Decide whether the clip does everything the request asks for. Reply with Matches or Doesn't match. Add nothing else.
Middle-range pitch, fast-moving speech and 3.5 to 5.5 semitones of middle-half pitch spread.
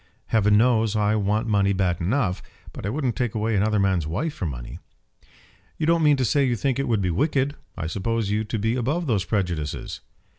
Doesn't match